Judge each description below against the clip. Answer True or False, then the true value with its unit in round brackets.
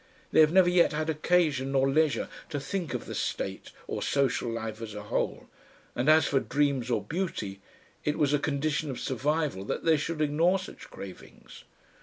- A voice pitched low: False (145 Hz)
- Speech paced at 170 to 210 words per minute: True (185 wpm)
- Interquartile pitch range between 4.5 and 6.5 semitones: False (3.3 semitones)